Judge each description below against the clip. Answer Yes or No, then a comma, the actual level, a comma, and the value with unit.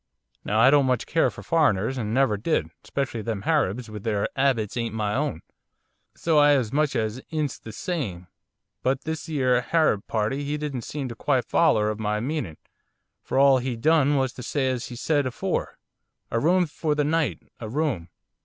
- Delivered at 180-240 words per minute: Yes, average, 190 wpm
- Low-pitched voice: Yes, low, 130 Hz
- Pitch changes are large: No, average, 4.9 semitones